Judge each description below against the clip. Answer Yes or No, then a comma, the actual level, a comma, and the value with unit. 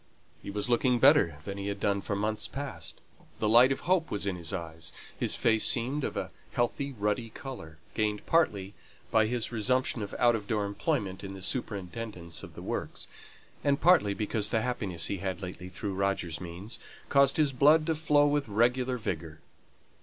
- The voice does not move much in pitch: No, average, 4.7 semitones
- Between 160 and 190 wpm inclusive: Yes, average, 185 wpm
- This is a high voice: No, low, 110 Hz